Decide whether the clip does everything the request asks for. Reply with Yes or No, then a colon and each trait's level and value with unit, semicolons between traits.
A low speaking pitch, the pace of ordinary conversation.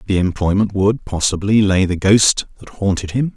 Yes: low, 100 Hz; average, 180 wpm